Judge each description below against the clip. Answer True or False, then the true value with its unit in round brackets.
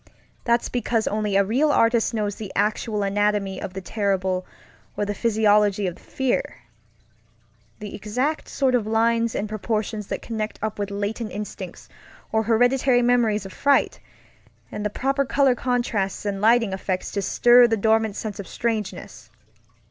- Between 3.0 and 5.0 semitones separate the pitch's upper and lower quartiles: False (2.6 semitones)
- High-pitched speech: True (215 Hz)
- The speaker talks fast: False (150 wpm)